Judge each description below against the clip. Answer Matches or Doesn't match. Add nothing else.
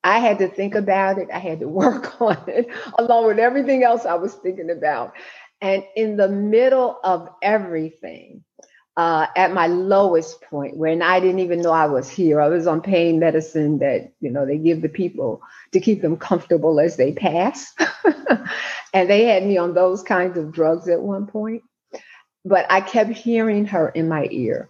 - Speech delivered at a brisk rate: Doesn't match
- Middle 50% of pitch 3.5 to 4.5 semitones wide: Matches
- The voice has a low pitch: Doesn't match